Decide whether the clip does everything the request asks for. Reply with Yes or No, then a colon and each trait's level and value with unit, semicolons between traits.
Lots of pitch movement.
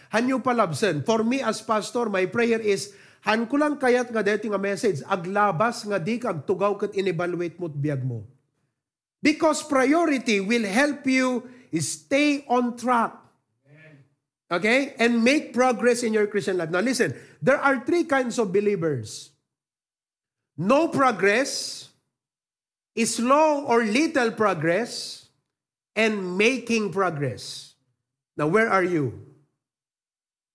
Yes: wide, 7.3 semitones